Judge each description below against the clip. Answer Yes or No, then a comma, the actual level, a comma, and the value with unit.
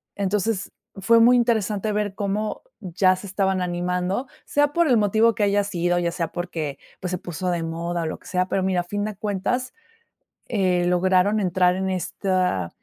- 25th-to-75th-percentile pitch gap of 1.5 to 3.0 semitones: Yes, average, 2.7 semitones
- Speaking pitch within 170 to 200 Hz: Yes, high, 190 Hz